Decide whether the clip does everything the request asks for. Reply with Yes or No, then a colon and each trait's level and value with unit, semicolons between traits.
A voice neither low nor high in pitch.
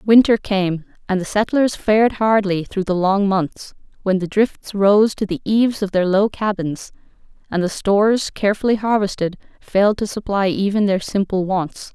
No: high, 200 Hz